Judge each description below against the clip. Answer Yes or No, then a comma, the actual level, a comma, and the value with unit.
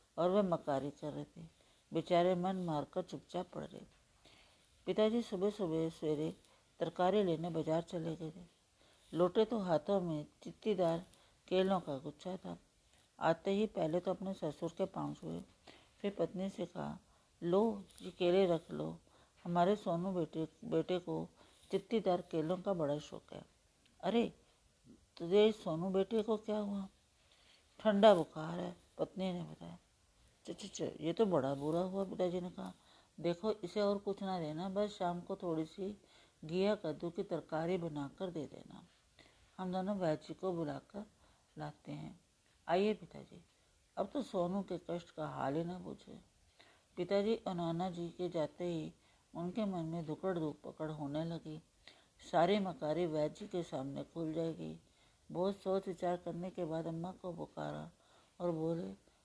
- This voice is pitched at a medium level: Yes, medium, 175 Hz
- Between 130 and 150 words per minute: No, average, 160 wpm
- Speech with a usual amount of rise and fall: Yes, average, 3.2 semitones